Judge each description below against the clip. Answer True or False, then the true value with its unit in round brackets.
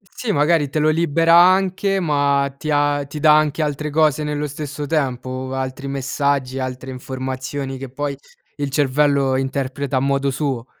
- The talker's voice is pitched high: False (140 Hz)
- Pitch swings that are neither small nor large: False (2.2 semitones)